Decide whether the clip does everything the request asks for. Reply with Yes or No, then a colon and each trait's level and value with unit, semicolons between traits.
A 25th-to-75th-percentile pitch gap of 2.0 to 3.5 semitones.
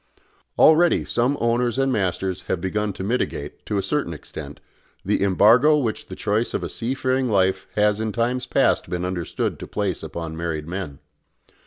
No: average, 5.2 semitones